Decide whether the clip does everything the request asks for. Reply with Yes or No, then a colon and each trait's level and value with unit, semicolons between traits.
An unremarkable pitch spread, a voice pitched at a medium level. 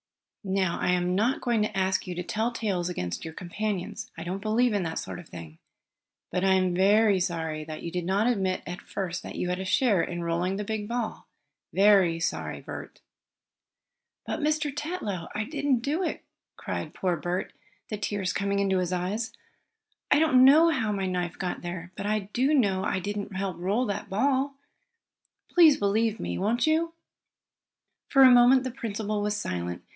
No: average, 4.6 semitones; high, 200 Hz